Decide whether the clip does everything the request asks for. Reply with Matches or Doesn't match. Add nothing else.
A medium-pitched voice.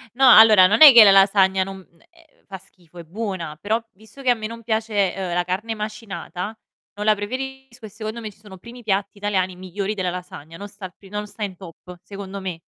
Doesn't match